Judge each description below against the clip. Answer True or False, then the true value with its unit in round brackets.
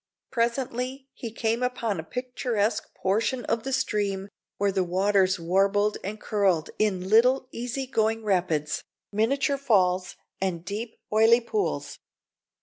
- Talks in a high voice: True (215 Hz)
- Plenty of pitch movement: False (4.1 semitones)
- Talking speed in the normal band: False (130 wpm)